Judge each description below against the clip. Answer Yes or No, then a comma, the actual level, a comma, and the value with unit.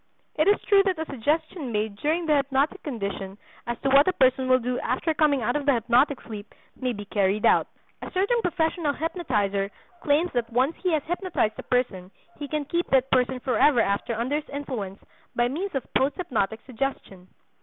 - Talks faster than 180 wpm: Yes, average, 195 wpm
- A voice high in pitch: Yes, very high, 265 Hz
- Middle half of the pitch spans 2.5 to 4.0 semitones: No, average, 5.1 semitones